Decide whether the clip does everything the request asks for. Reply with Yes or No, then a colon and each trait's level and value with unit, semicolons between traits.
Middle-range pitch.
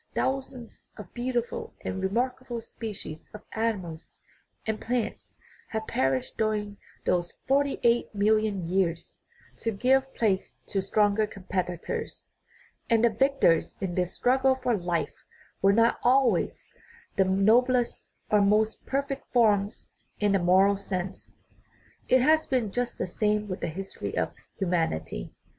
No: high, 215 Hz